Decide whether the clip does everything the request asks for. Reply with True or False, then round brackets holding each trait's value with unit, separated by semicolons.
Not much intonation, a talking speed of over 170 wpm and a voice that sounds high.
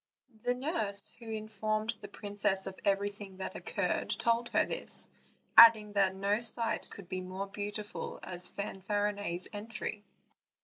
False (1.8 semitones; 135 wpm; 205 Hz)